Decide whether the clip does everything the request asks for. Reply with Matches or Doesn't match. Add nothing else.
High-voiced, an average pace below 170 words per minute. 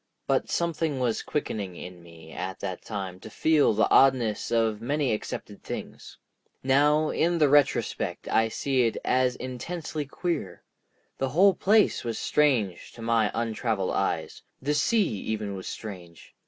Doesn't match